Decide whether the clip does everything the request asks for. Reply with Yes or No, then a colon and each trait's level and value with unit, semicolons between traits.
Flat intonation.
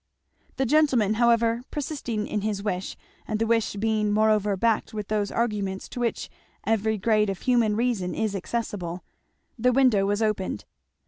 Yes: narrow, 2.3 semitones